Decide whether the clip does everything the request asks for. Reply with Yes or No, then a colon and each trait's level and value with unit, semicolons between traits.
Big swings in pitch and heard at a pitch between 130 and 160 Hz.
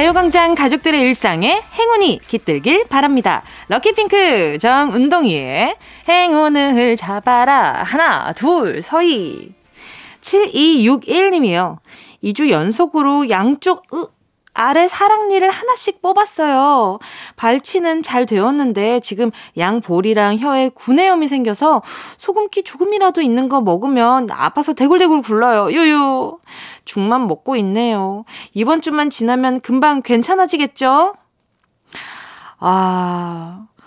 No: wide, 6.8 semitones; very high, 280 Hz